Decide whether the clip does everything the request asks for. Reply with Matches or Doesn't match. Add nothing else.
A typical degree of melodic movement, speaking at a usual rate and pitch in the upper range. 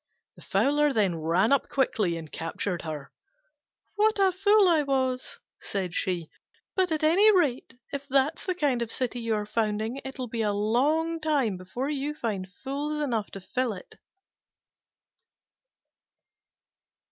Doesn't match